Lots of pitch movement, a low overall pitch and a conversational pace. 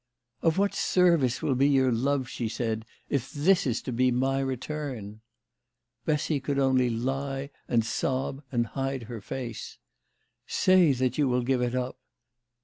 No: narrow, 2.6 semitones; low, 130 Hz; average, 170 wpm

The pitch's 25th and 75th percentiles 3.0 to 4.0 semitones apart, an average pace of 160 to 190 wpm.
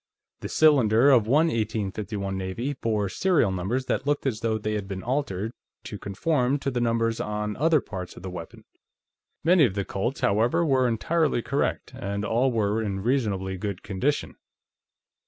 No: average, 4.9 semitones; average, 170 wpm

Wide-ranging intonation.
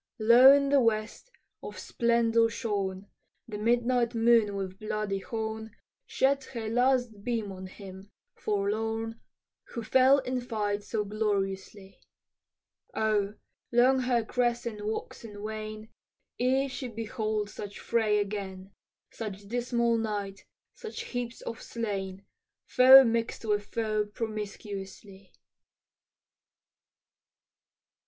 No: narrow, 2.6 semitones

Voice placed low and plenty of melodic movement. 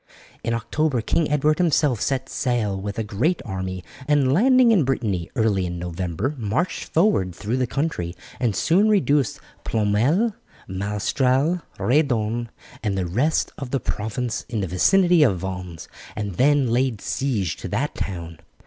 Yes: low, 120 Hz; wide, 7.0 semitones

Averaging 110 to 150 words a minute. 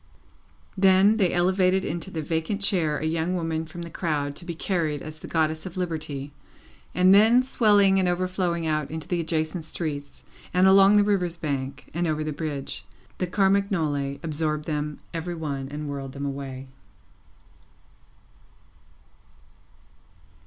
Yes: average, 145 wpm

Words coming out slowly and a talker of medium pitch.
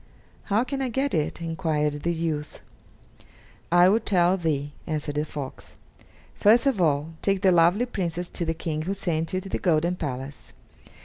No: average, 175 wpm; medium, 170 Hz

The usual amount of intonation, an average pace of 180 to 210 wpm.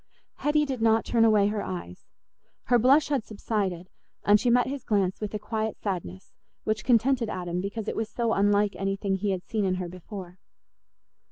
Yes: average, 3.3 semitones; average, 185 wpm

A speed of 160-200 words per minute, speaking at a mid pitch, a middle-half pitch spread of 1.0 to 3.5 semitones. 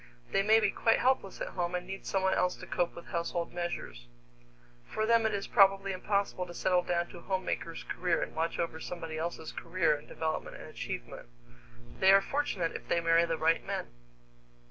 Yes: average, 195 wpm; medium, 180 Hz; average, 2.8 semitones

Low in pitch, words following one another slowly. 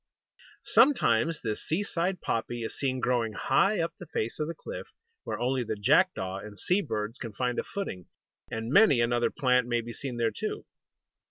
No: low, 120 Hz; average, 180 wpm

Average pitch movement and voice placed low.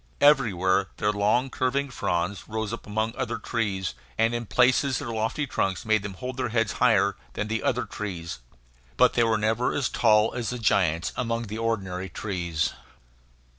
Yes: average, 3.3 semitones; low, 110 Hz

